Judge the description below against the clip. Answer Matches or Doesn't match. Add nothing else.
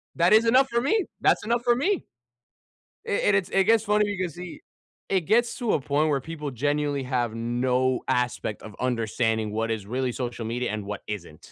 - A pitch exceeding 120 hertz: Matches